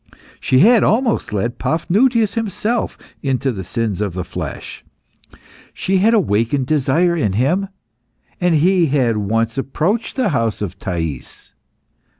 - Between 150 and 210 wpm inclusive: No, slow, 135 wpm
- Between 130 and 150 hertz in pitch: Yes, medium, 140 Hz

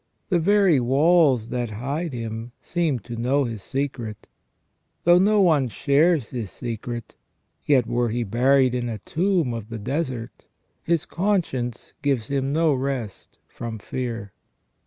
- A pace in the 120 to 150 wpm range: Yes, average, 140 wpm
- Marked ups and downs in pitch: No, average, 5.0 semitones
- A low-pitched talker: Yes, low, 130 Hz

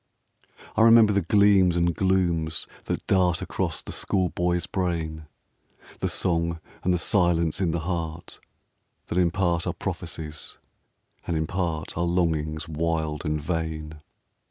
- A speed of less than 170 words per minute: Yes, average, 140 wpm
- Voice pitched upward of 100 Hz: No, very low, 85 Hz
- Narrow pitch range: Yes, narrow, 2.3 semitones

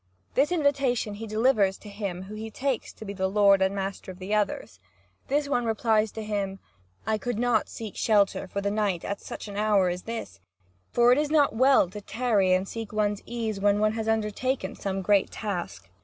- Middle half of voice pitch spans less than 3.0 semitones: Yes, narrow, 2.6 semitones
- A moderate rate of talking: No, fast, 210 wpm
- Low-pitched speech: No, high, 210 Hz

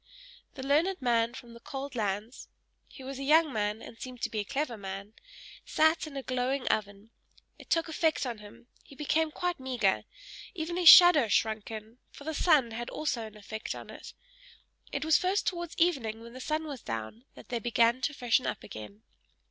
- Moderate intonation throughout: No, wide, 5.7 semitones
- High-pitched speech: Yes, very high, 255 Hz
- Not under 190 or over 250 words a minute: Yes, average, 195 wpm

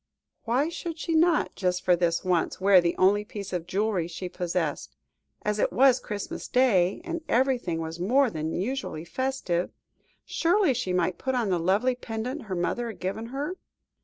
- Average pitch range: No, wide, 6.4 semitones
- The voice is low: No, high, 205 Hz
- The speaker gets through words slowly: No, average, 175 wpm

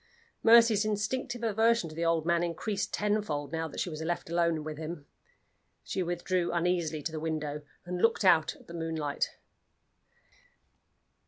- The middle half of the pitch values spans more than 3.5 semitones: Yes, average, 4.4 semitones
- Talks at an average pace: Yes, average, 155 wpm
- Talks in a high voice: No, medium, 170 Hz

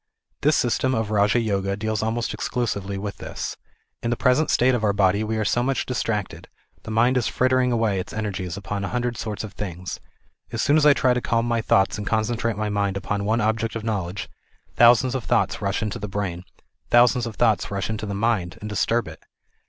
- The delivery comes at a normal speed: No, fast, 215 wpm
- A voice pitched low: Yes, low, 110 Hz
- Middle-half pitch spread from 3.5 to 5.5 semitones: No, average, 2.9 semitones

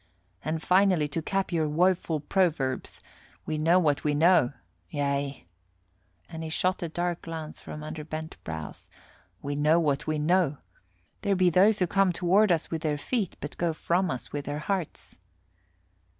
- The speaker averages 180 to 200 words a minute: No, average, 165 wpm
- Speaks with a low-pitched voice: No, medium, 160 Hz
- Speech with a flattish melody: No, average, 3.4 semitones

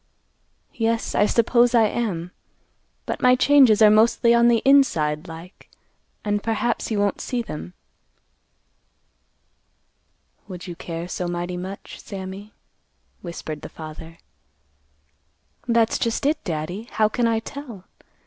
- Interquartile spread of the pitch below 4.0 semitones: No, average, 4.9 semitones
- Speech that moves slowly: Yes, slow, 125 wpm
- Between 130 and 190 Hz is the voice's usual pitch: No, high, 210 Hz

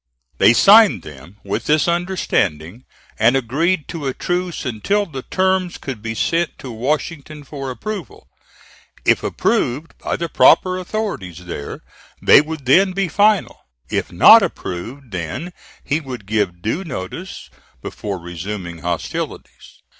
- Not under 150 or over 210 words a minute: No, slow, 135 wpm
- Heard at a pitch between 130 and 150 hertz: Yes, low, 135 Hz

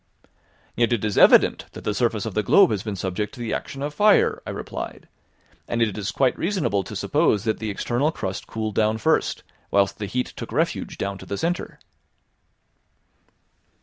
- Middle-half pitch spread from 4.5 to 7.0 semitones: No, average, 3.8 semitones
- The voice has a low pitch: Yes, low, 110 Hz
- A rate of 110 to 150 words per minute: No, average, 185 wpm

